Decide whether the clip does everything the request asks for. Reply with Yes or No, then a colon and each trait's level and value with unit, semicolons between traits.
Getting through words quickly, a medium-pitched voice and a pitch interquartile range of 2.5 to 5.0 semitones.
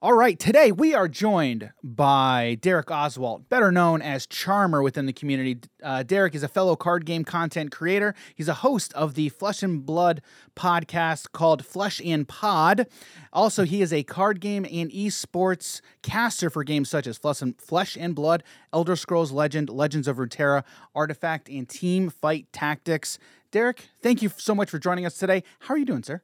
No: average, 185 wpm; medium, 165 Hz; average, 4.6 semitones